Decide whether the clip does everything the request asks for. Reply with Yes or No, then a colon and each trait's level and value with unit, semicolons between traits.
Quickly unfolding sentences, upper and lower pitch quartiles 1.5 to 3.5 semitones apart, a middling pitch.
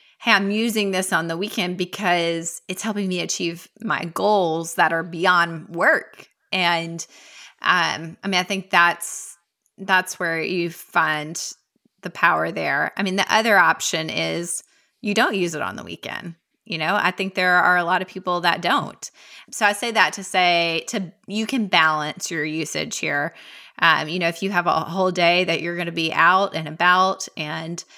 No: average, 190 wpm; narrow, 2.6 semitones; medium, 180 Hz